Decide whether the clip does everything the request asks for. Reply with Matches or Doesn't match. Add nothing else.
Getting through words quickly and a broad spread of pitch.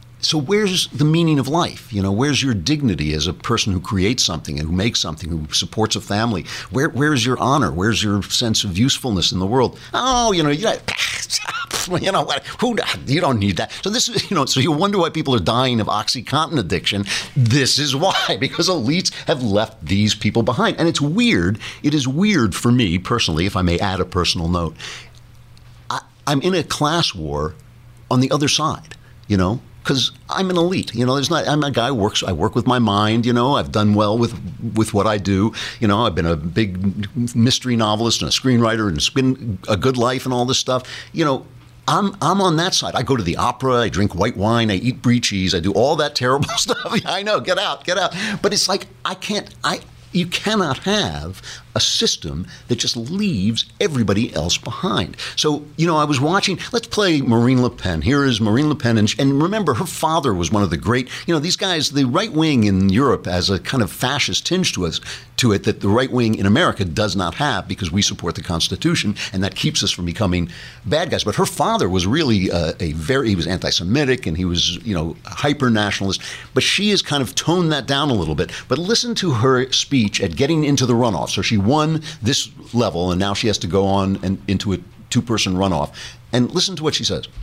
Matches